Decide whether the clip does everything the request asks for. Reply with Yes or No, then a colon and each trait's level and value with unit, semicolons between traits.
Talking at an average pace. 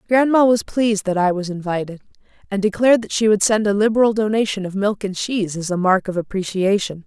No: fast, 210 wpm